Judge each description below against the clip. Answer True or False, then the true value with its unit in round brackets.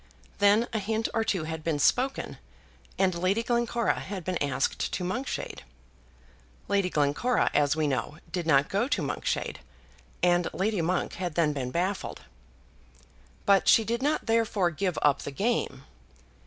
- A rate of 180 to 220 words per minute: False (155 wpm)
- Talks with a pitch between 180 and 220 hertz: True (185 Hz)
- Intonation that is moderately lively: False (6.0 semitones)